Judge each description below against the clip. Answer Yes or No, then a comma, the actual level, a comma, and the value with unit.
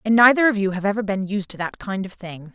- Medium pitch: No, high, 200 Hz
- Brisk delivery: Yes, fast, 305 wpm